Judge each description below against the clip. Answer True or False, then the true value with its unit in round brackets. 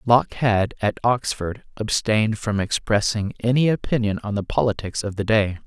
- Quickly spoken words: False (160 wpm)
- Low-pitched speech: True (110 Hz)